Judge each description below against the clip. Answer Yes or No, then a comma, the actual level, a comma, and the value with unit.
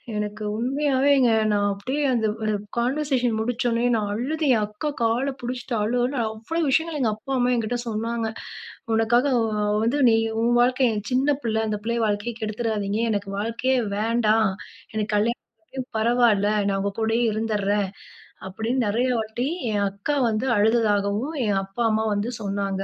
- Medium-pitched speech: No, high, 225 Hz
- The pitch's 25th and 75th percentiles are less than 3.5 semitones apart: Yes, average, 2.8 semitones